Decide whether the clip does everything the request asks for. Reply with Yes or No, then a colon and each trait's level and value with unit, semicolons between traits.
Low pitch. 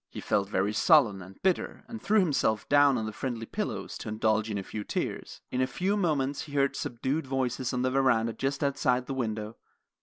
Yes: low, 130 Hz